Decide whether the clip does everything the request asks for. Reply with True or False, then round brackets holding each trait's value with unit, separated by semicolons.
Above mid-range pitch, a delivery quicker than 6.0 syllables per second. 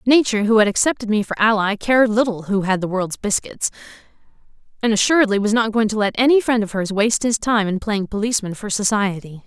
True (215 Hz; 6.2 syllables/s)